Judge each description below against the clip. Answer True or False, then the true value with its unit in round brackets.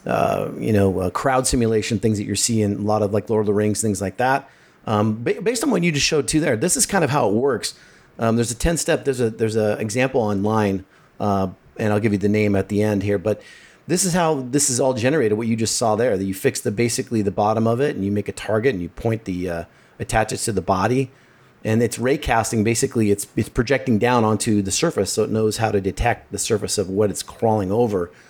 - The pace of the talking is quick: True (255 wpm)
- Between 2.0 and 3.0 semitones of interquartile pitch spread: False (3.8 semitones)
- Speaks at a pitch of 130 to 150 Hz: False (110 Hz)